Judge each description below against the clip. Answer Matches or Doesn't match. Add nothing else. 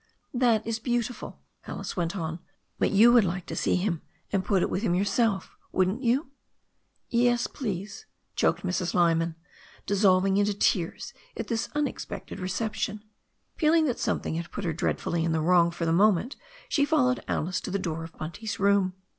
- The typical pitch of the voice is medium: Doesn't match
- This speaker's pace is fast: Doesn't match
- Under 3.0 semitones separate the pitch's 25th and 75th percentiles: Doesn't match